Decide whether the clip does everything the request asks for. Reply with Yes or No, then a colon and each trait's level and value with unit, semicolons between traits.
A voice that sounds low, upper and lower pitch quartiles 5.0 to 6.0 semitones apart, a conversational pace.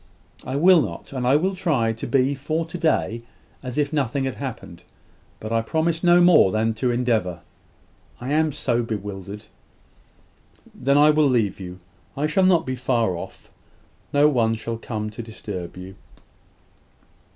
Yes: low, 125 Hz; average, 5.3 semitones; average, 165 wpm